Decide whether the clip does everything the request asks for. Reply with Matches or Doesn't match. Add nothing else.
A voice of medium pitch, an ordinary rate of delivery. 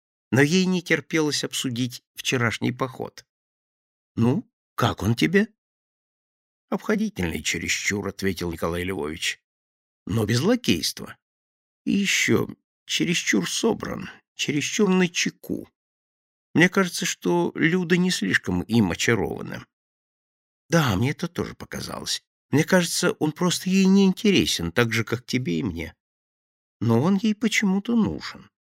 Matches